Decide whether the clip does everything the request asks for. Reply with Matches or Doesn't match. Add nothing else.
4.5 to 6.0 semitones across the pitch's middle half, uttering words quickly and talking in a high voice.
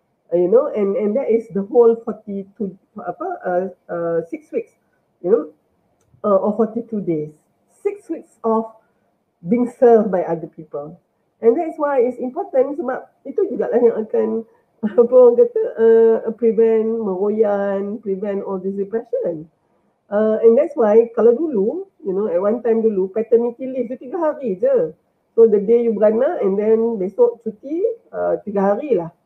Matches